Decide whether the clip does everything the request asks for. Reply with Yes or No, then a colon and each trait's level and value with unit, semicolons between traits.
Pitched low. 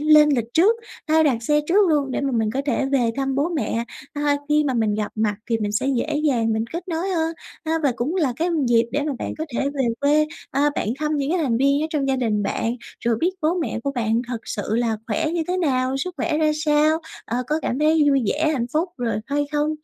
No: very high, 280 Hz